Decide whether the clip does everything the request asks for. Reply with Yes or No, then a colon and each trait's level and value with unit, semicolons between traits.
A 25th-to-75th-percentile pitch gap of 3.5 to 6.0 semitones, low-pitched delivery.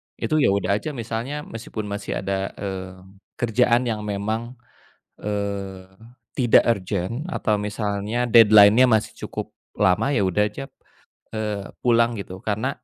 No: average, 2.7 semitones; low, 105 Hz